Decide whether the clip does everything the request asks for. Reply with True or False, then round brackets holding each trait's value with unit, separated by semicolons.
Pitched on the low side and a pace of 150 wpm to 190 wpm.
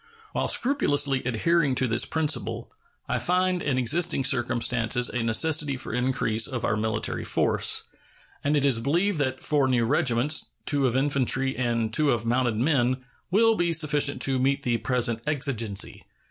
True (130 Hz; 160 wpm)